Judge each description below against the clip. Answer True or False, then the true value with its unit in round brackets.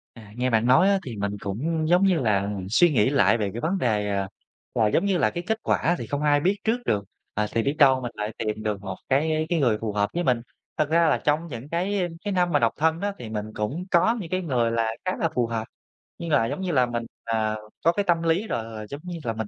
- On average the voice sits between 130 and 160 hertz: True (135 Hz)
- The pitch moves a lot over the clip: True (7.4 semitones)